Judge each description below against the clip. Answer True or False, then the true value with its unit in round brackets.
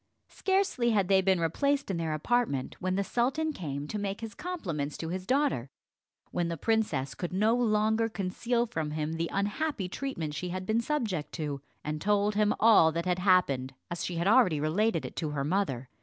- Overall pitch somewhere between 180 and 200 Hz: True (190 Hz)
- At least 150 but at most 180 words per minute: False (195 wpm)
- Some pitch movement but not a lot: False (6.0 semitones)